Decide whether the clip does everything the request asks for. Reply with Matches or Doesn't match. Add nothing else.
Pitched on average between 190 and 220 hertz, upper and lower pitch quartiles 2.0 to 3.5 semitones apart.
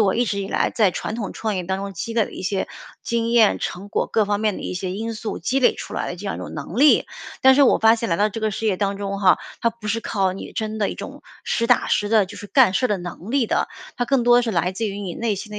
Matches